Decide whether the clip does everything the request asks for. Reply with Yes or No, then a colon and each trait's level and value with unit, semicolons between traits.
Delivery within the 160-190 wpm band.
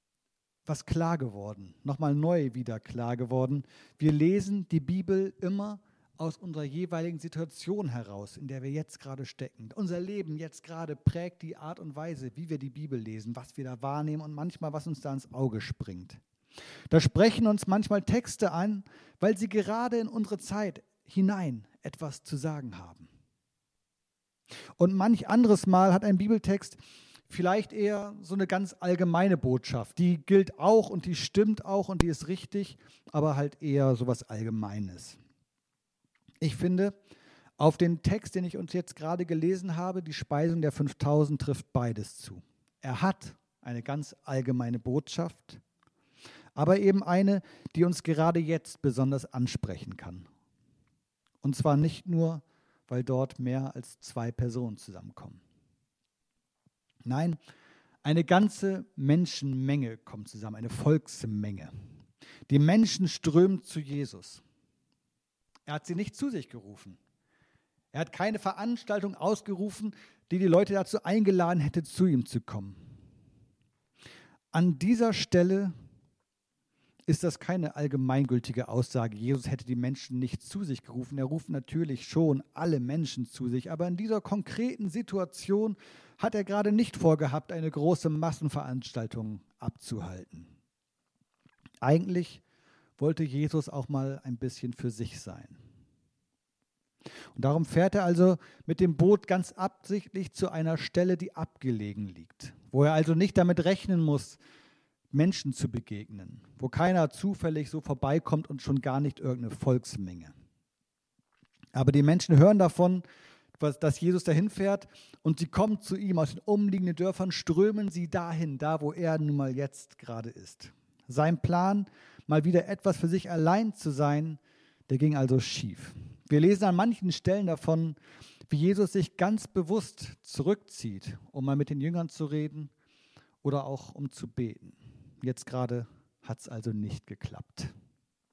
No: average, 145 wpm